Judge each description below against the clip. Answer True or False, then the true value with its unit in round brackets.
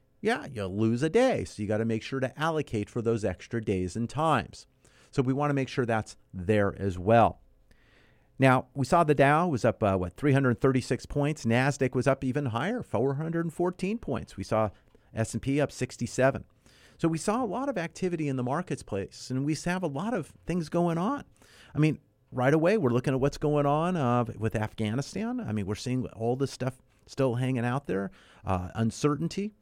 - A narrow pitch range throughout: False (5.2 semitones)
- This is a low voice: True (130 Hz)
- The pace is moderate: True (195 wpm)